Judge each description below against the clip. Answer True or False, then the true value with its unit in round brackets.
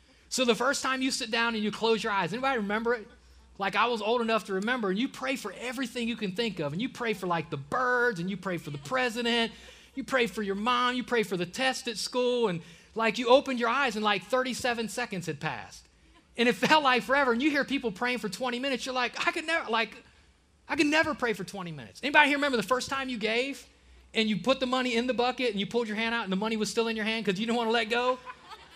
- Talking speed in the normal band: False (275 wpm)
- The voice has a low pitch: False (235 Hz)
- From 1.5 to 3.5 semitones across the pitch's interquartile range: True (3.1 semitones)